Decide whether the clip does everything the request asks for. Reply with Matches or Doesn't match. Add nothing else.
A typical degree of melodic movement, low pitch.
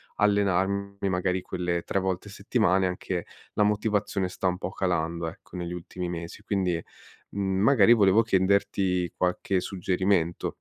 Doesn't match